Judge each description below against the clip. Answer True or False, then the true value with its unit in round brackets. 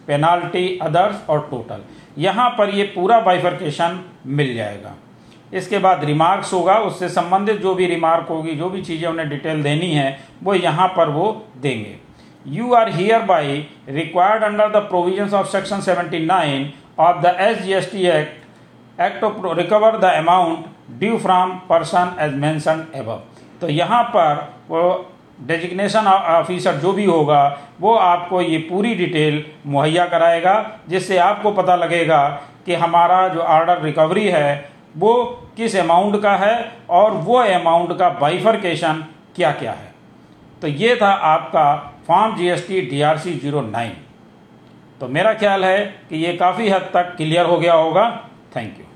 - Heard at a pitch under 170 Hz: False (175 Hz)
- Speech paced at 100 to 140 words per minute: False (155 wpm)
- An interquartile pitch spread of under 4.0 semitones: True (3.5 semitones)